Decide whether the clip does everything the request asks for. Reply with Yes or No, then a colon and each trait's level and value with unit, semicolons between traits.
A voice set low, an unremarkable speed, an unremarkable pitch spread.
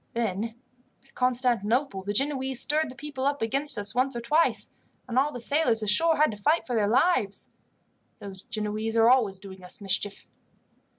No: high, 235 Hz; average, 175 wpm; average, 4.7 semitones